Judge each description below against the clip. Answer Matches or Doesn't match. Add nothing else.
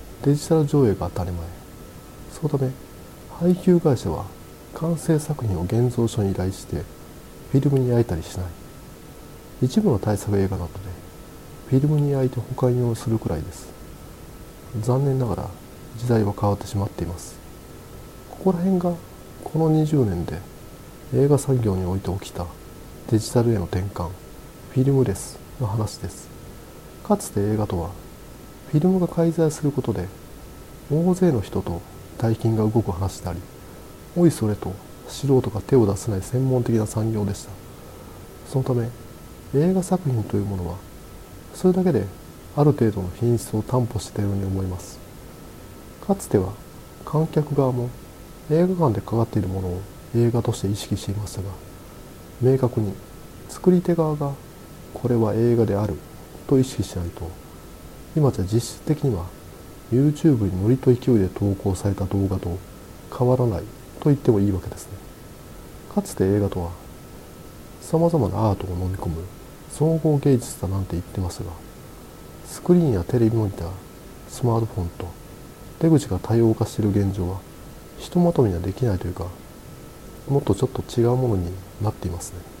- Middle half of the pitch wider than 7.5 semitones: Doesn't match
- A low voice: Matches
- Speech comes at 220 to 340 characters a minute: Matches